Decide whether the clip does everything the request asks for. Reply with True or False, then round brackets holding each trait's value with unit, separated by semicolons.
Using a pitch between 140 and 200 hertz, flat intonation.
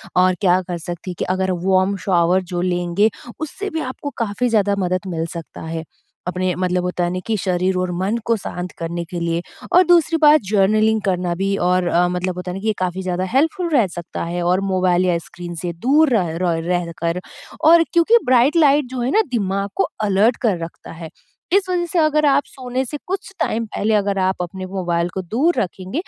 False (190 Hz; 5.3 semitones)